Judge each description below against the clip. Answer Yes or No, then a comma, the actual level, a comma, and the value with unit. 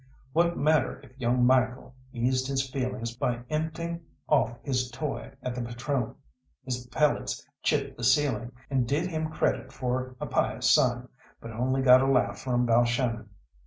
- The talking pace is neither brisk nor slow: Yes, average, 160 wpm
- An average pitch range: No, narrow, 2.2 semitones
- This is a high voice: No, low, 130 Hz